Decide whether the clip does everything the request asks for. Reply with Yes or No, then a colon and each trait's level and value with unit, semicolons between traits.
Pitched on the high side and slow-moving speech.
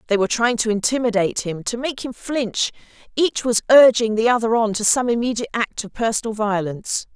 No: high, 225 Hz; average, 185 wpm